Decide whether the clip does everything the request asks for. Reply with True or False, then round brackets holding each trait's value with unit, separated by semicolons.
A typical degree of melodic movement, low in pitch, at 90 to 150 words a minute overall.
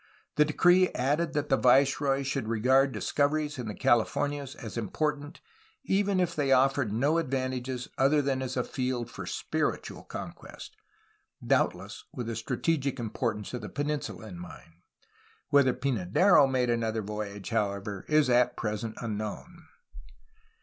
True (4.2 semitones; 130 Hz; 145 wpm)